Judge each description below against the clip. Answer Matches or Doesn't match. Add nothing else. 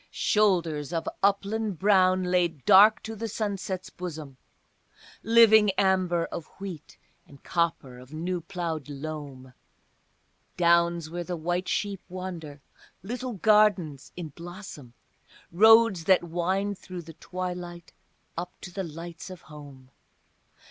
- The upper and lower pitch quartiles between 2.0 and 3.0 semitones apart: Doesn't match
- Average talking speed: Doesn't match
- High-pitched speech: Doesn't match